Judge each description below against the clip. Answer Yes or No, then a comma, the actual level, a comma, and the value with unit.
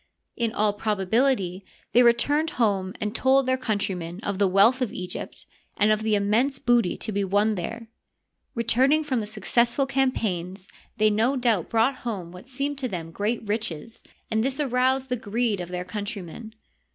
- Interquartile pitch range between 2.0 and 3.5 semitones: No, average, 4.1 semitones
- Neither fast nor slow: Yes, average, 170 wpm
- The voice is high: Yes, high, 220 Hz